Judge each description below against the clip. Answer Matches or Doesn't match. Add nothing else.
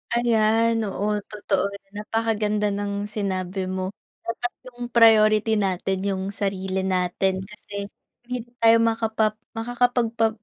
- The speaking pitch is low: Doesn't match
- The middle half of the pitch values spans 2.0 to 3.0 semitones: Matches